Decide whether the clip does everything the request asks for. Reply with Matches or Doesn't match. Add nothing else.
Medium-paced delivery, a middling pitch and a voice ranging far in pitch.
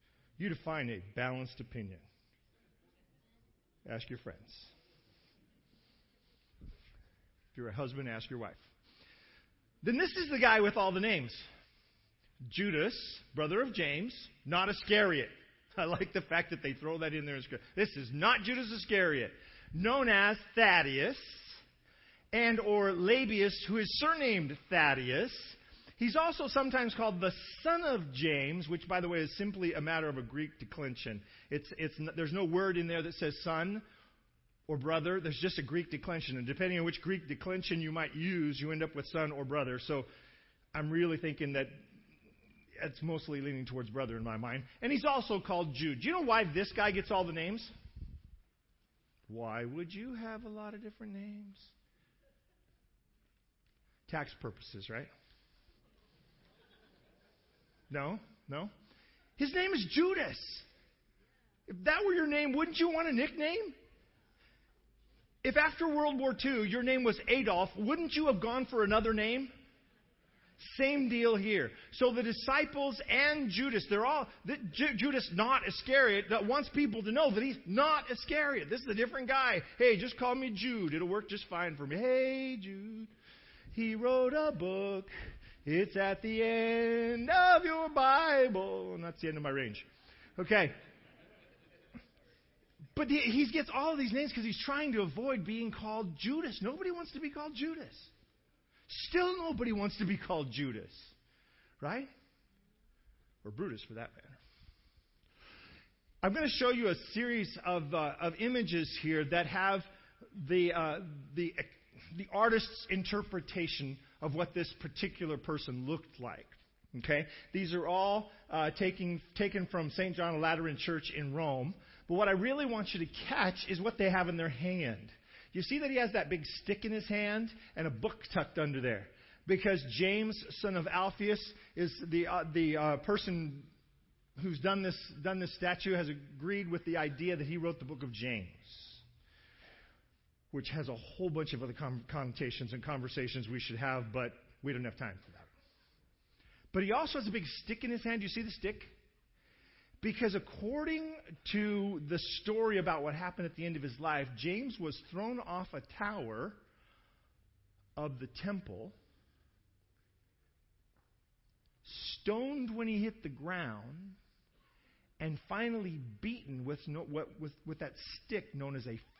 Matches